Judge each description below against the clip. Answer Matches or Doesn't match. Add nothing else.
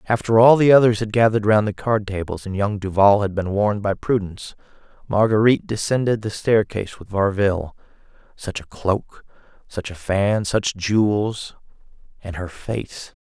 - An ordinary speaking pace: Matches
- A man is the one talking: Matches